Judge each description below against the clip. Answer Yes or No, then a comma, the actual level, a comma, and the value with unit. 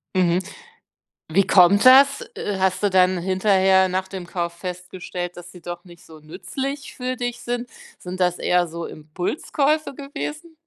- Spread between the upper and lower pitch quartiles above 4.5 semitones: Yes, wide, 5.5 semitones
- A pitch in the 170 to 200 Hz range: Yes, medium, 185 Hz